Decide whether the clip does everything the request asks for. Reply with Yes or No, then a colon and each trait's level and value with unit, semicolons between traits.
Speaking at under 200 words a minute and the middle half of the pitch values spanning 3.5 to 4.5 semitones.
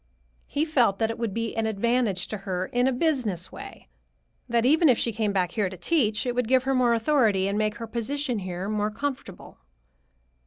No: fast, 205 wpm; average, 3.9 semitones